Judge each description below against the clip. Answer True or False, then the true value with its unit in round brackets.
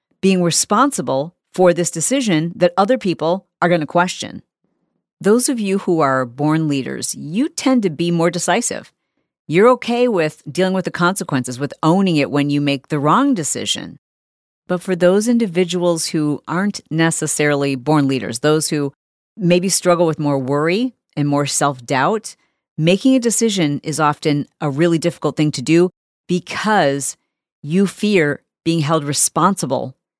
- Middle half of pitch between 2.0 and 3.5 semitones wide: False (4.2 semitones)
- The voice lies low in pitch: False (170 Hz)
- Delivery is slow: False (155 wpm)